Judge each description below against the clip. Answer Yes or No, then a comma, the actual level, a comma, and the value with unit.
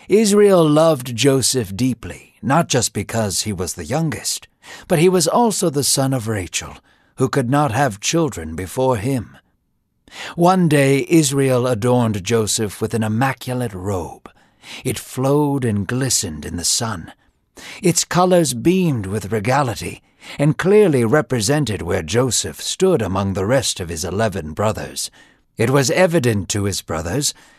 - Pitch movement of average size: No, wide, 6.4 semitones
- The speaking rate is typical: Yes, average, 145 wpm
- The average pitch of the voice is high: No, low, 125 Hz